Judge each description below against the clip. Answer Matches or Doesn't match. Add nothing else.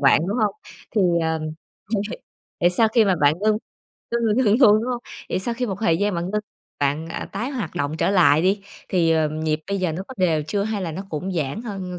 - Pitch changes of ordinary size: Matches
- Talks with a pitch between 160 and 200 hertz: Matches